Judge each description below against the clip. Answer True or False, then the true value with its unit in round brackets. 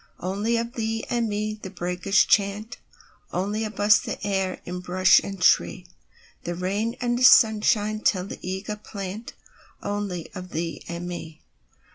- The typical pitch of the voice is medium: False (205 Hz)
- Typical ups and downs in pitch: True (3.0 semitones)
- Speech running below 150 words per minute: True (135 wpm)